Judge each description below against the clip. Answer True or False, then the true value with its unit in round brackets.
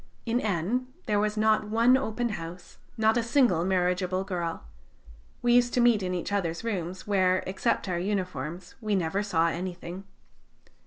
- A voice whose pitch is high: True (195 Hz)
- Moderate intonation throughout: True (3.7 semitones)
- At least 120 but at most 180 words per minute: True (160 wpm)